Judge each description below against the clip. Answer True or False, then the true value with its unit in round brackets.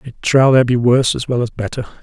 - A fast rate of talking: True (265 wpm)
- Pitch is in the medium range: False (125 Hz)